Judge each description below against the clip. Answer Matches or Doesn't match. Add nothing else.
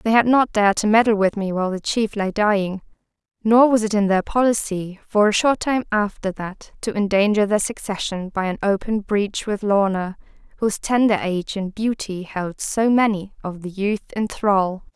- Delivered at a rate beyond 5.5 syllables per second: Doesn't match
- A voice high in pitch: Matches